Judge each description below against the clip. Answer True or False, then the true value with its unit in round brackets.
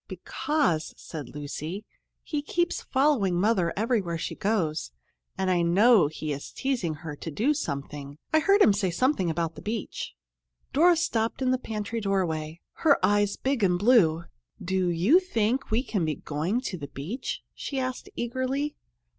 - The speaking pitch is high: True (205 Hz)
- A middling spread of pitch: False (7.6 semitones)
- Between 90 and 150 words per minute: False (165 wpm)